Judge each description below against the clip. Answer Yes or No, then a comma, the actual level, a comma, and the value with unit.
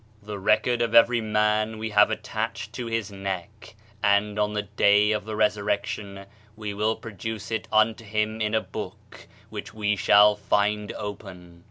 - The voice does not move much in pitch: Yes, narrow, 1.1 semitones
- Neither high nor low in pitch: No, low, 105 Hz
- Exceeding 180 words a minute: No, average, 165 wpm